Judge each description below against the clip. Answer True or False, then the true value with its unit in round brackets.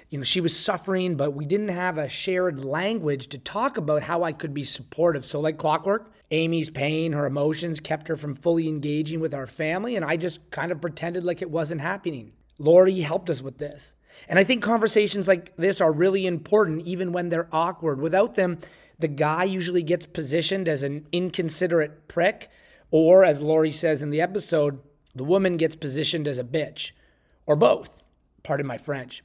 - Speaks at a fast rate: False (190 wpm)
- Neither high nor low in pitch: True (165 Hz)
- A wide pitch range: False (3.2 semitones)